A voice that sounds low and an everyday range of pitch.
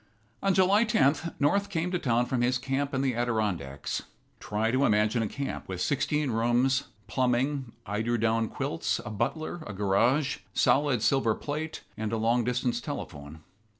Yes: low, 125 Hz; average, 4.3 semitones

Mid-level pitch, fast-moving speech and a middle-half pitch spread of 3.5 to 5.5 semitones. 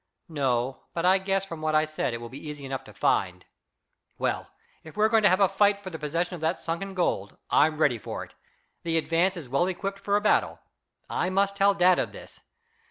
Yes: medium, 175 Hz; fast, 225 wpm; average, 4.1 semitones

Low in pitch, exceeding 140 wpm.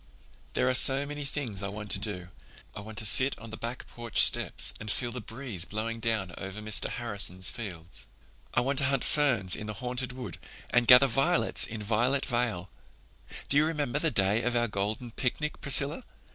Yes: low, 120 Hz; average, 195 wpm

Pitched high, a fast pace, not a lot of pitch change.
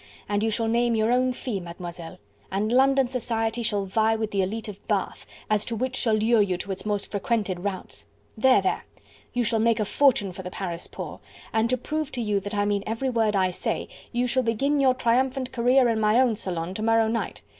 No: high, 225 Hz; fast, 220 wpm; average, 3.2 semitones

